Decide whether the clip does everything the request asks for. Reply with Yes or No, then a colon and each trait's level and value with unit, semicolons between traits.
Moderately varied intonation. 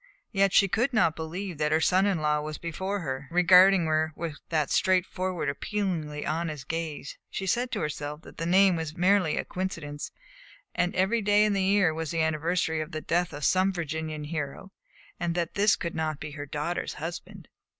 Yes: average, 3.5 semitones